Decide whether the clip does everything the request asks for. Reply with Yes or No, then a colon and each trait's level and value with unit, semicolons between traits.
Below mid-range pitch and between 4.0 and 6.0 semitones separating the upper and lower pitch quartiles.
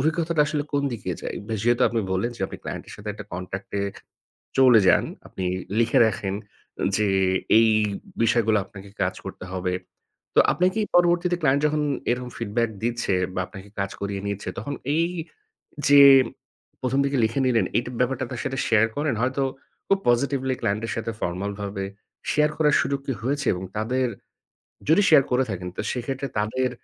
Yes: low, 120 Hz; wide, 5.4 semitones